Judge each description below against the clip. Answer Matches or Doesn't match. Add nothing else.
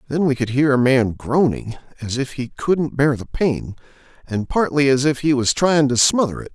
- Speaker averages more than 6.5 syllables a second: Doesn't match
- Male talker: Matches